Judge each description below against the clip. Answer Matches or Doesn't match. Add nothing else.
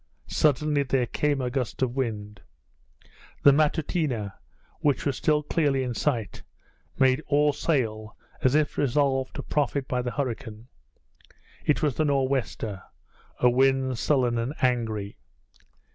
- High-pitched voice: Doesn't match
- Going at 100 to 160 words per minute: Matches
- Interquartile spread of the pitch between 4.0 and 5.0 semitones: Doesn't match